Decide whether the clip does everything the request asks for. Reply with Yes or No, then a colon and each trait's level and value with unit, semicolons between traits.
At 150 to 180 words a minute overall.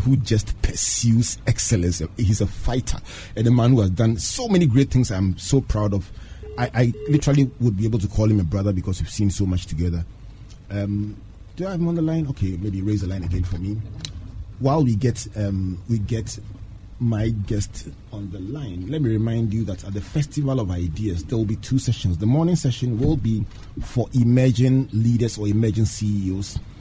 No: fast, 205 wpm